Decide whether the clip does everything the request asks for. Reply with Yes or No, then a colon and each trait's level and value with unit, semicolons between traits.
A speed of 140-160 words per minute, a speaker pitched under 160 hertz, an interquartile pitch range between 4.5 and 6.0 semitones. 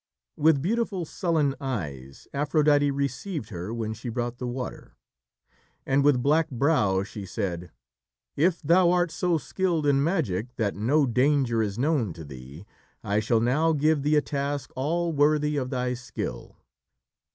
Yes: average, 150 wpm; medium, 140 Hz; average, 5.3 semitones